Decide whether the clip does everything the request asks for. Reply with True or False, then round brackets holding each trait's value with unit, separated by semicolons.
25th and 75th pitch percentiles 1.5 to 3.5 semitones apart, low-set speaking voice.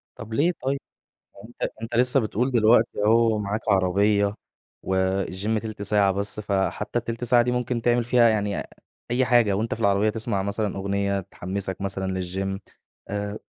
True (2.9 semitones; 105 Hz)